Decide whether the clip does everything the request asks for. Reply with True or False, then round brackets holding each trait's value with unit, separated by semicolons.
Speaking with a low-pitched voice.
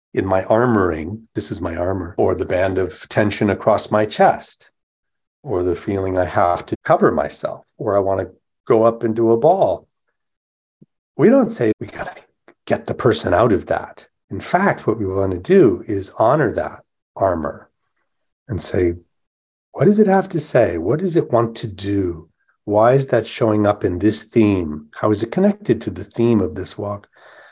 True (105 Hz)